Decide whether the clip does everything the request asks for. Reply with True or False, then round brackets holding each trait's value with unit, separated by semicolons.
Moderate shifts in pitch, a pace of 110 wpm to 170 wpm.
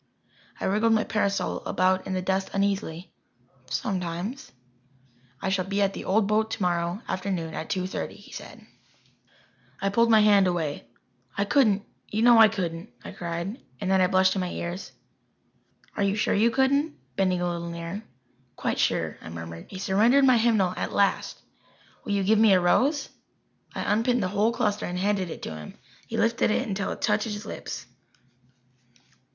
False (3.2 semitones; 180 wpm)